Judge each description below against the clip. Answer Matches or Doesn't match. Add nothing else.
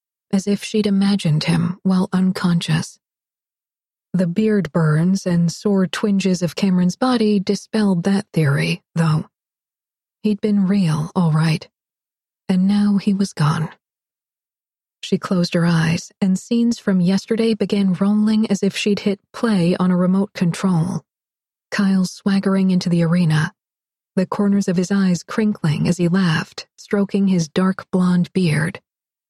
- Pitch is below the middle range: Doesn't match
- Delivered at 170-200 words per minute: Doesn't match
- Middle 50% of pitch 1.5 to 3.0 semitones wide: Matches